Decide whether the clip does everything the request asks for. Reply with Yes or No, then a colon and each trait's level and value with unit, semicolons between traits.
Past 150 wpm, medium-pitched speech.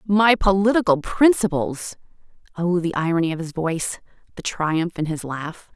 No: average, 145 wpm; medium, 175 Hz